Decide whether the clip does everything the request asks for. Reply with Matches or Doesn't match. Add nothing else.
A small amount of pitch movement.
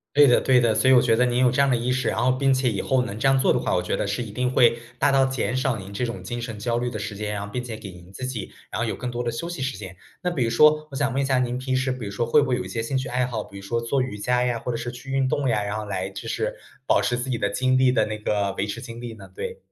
Doesn't match